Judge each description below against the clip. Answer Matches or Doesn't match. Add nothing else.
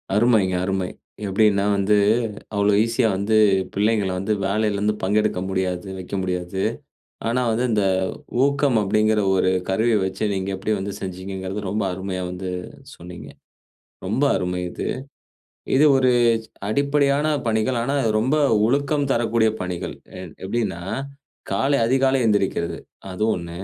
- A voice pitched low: Matches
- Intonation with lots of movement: Doesn't match